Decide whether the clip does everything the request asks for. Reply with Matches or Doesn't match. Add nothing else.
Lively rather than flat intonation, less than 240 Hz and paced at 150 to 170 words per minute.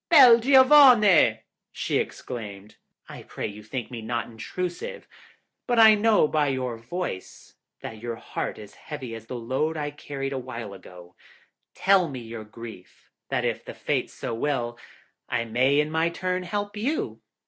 Matches